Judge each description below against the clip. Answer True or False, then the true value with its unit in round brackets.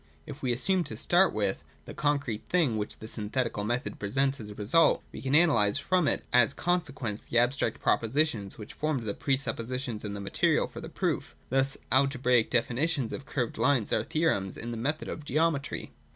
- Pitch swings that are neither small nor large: True (4.7 semitones)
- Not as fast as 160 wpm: False (195 wpm)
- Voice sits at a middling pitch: False (130 Hz)